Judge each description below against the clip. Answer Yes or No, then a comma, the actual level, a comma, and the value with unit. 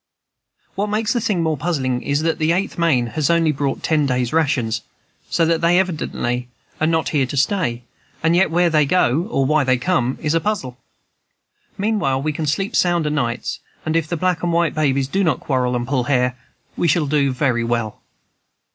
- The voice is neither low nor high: Yes, medium, 155 Hz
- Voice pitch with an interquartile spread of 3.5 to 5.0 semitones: Yes, average, 4.7 semitones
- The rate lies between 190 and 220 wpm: Yes, average, 200 wpm